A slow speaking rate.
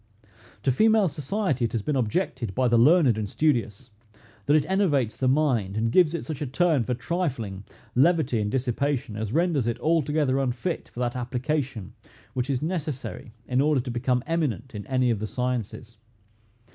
No: average, 175 wpm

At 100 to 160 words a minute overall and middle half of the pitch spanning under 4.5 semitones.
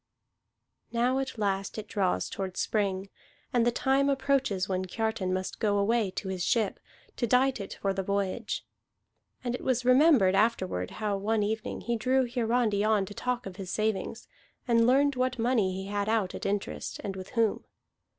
No: average, 180 wpm; average, 4.0 semitones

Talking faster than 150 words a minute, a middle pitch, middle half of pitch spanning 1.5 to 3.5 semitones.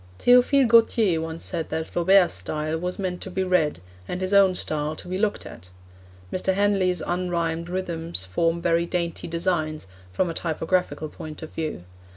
Yes: average, 170 wpm; medium, 170 Hz; narrow, 2.5 semitones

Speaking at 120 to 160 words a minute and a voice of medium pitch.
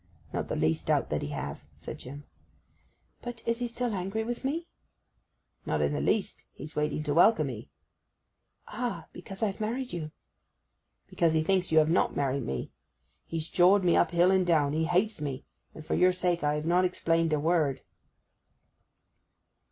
No: average, 175 wpm; medium, 170 Hz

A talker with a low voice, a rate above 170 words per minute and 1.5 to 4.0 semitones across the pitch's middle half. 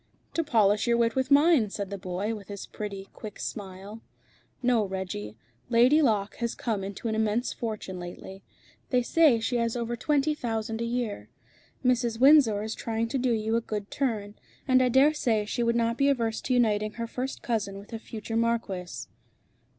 No: high, 225 Hz; average, 190 wpm; average, 3.1 semitones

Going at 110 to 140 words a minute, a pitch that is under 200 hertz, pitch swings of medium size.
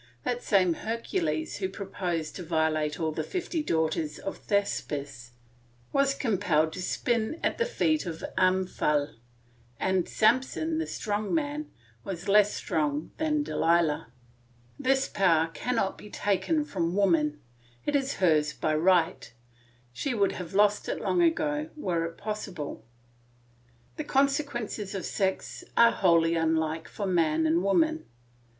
No: slow, 135 wpm; high, 190 Hz; wide, 7.1 semitones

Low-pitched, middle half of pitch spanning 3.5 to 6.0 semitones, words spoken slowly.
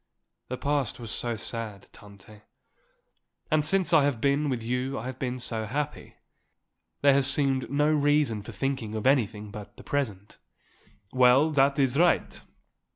No: low, 130 Hz; average, 4.2 semitones; average, 155 wpm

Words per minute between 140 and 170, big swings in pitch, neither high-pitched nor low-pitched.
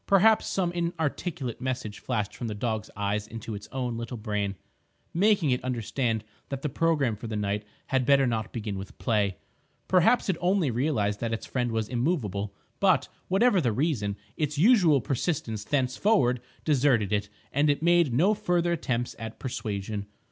No: average, 165 wpm; wide, 6.9 semitones; low, 125 Hz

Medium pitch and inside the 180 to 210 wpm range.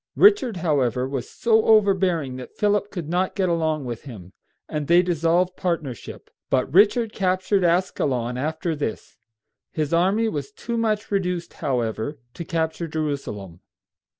No: medium, 170 Hz; average, 140 wpm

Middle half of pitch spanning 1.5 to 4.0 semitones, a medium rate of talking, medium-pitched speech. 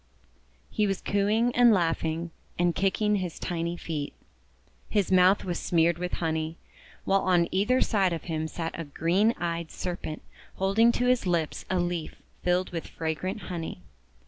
Yes: average, 2.9 semitones; average, 160 wpm; medium, 175 Hz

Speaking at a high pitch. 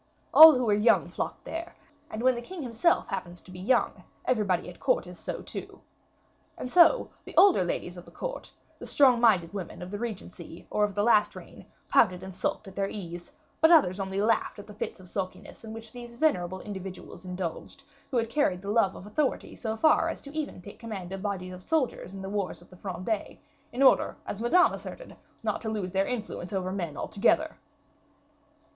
Yes: high, 205 Hz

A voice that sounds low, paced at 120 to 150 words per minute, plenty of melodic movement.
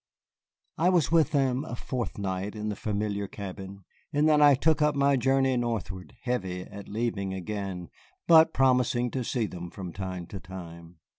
No: low, 110 Hz; average, 165 wpm; wide, 6.0 semitones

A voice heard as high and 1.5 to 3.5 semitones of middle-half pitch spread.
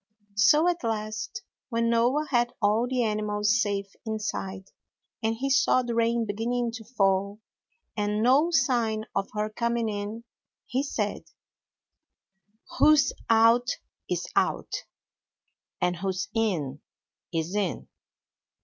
Yes: high, 225 Hz; average, 2.8 semitones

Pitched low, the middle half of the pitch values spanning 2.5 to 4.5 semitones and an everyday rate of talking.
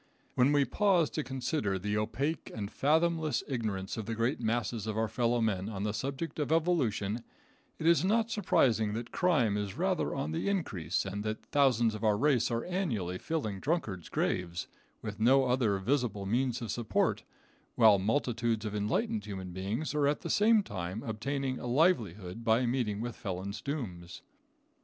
No: low, 115 Hz; wide, 5.5 semitones; average, 170 wpm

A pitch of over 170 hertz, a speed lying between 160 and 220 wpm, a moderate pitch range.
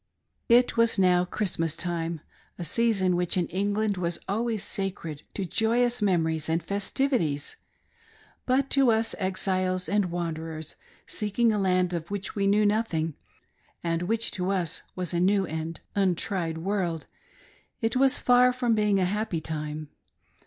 No: high, 190 Hz; average, 150 wpm; average, 4.2 semitones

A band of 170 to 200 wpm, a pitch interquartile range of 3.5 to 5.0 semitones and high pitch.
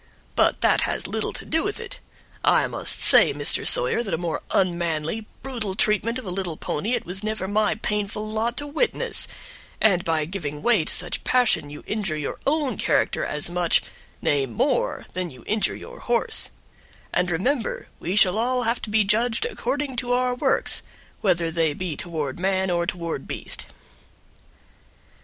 No: average, 175 wpm; wide, 5.6 semitones; high, 200 Hz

